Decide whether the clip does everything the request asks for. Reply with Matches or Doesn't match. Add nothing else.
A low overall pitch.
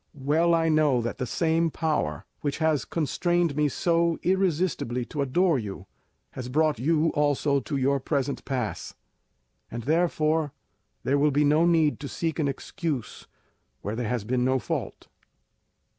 Doesn't match